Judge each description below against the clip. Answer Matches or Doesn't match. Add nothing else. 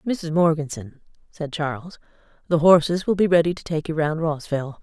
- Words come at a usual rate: Matches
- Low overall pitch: Doesn't match